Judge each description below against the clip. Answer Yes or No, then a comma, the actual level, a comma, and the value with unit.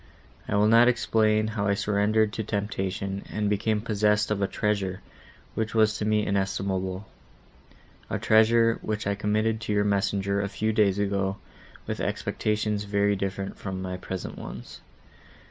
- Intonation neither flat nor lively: No, narrow, 1.6 semitones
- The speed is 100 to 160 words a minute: Yes, average, 155 wpm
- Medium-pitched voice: No, low, 105 Hz